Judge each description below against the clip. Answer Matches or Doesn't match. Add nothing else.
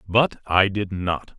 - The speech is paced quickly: Doesn't match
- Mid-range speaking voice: Doesn't match